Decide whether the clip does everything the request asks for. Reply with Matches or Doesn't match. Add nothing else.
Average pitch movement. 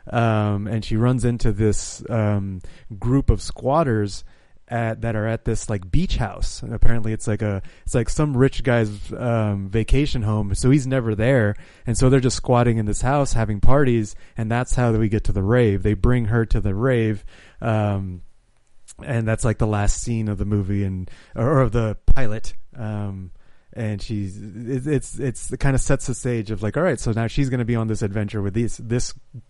Matches